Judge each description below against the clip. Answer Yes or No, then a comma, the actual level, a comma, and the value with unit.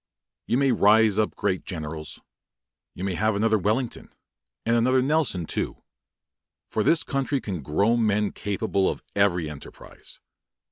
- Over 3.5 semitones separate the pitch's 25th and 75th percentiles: Yes, average, 4.1 semitones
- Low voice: Yes, low, 105 Hz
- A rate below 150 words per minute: Yes, average, 140 wpm